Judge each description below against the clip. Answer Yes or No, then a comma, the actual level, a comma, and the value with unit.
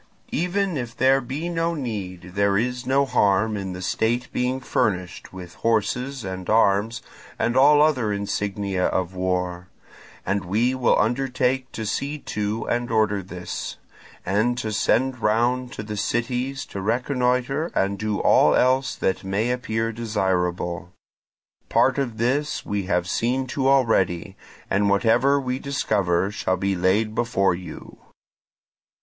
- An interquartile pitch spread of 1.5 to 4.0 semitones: No, average, 4.7 semitones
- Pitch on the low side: Yes, low, 110 Hz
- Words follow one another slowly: No, average, 145 wpm